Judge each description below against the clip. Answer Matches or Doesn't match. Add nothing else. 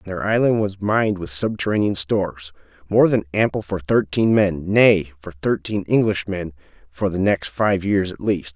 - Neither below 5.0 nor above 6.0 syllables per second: Doesn't match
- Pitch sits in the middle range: Doesn't match